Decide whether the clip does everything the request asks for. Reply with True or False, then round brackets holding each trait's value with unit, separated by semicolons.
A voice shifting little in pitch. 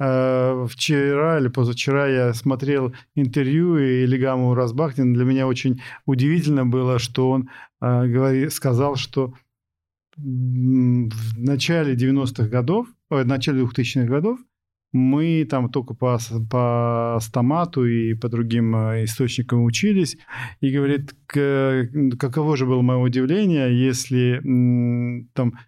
True (2.1 semitones)